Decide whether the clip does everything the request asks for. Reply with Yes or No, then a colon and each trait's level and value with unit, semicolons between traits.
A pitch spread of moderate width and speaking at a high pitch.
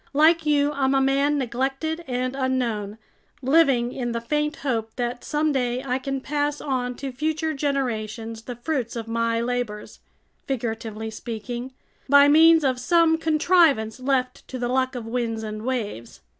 Yes: average, 3.6 semitones; very high, 255 Hz